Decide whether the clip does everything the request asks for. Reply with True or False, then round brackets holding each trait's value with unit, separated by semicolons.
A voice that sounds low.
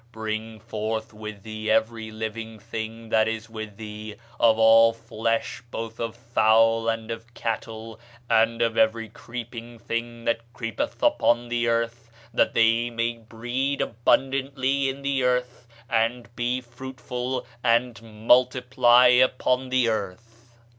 True (115 Hz)